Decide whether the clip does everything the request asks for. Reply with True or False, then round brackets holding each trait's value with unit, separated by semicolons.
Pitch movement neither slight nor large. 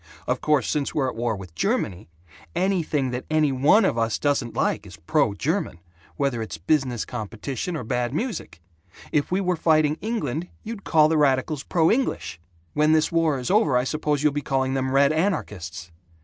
True (4.6 semitones)